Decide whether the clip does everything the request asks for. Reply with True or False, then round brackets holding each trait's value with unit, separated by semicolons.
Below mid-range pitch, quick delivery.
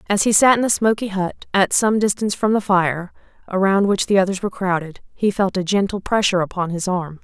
False (195 Hz; 225 wpm)